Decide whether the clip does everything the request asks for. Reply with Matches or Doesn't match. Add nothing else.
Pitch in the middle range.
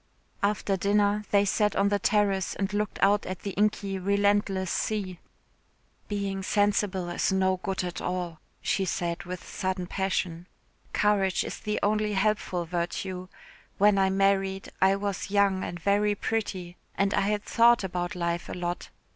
Doesn't match